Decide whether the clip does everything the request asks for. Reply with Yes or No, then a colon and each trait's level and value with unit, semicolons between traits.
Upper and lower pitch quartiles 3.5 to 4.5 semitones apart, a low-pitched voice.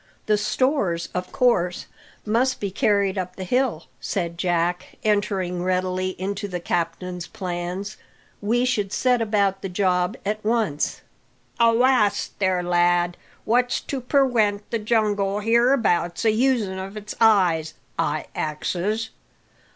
No: average, 3.8 semitones; high, 200 Hz